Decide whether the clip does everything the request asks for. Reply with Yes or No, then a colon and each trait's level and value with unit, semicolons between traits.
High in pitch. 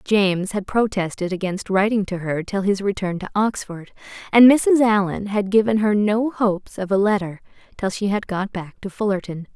Yes: high, 200 Hz